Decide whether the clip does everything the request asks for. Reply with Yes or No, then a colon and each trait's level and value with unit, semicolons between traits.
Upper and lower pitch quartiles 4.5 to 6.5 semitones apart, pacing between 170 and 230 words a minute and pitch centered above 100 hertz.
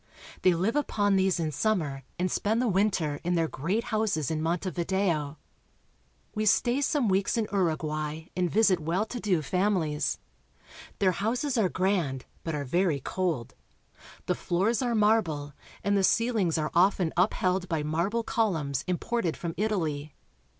No: average, 5.0 semitones; average, 155 wpm; medium, 185 Hz